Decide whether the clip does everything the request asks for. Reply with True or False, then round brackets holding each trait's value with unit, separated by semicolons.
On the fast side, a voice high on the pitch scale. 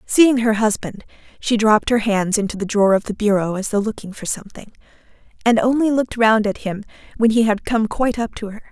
True (220 wpm; 220 Hz)